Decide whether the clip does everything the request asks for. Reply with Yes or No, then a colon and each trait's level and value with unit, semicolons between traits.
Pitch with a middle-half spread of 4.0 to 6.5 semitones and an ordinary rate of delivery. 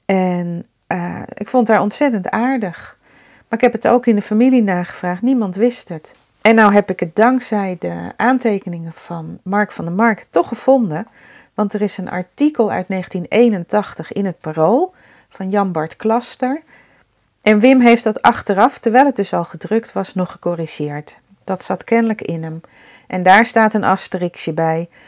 Yes: average, 4.7 semitones; average, 170 wpm